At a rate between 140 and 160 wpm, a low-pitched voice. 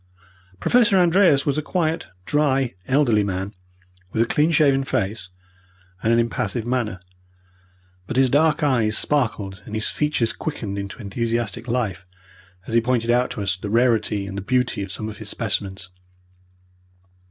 Yes: average, 155 wpm; low, 115 Hz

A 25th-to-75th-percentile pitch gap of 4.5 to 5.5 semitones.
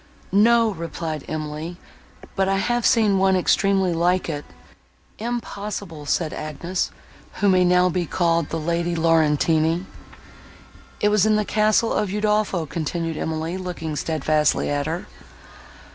No: average, 3.8 semitones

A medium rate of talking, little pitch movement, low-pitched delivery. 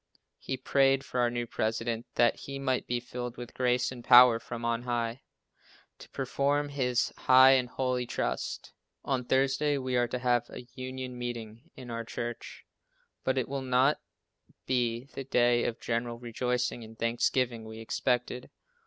Yes: average, 160 wpm; narrow, 1.6 semitones; low, 125 Hz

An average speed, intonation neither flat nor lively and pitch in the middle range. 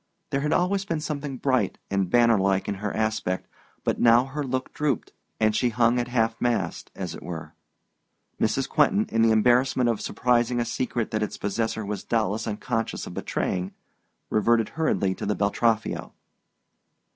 No: average, 165 wpm; average, 3.3 semitones; low, 115 Hz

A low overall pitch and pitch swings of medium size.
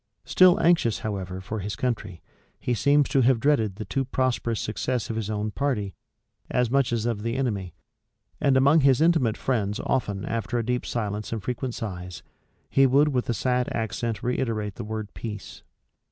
Yes: low, 115 Hz; average, 3.8 semitones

